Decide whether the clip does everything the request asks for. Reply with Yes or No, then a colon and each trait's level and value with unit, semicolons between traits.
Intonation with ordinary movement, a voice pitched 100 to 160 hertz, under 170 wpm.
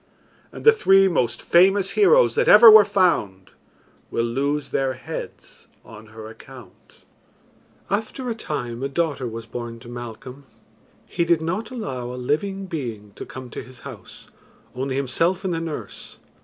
No: wide, 8.1 semitones; medium, 140 Hz; average, 155 wpm